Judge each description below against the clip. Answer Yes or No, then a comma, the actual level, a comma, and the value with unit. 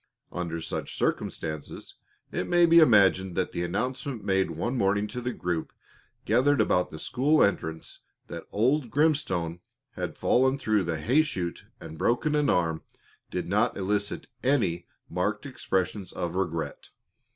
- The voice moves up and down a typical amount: No, wide, 6.6 semitones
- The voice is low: Yes, low, 100 Hz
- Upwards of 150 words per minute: No, average, 145 wpm